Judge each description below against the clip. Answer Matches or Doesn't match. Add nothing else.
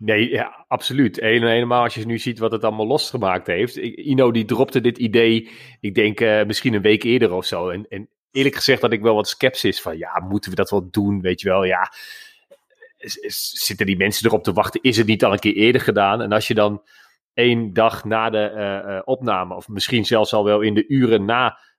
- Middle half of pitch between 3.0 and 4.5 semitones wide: Doesn't match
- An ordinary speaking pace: Doesn't match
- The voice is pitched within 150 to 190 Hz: Doesn't match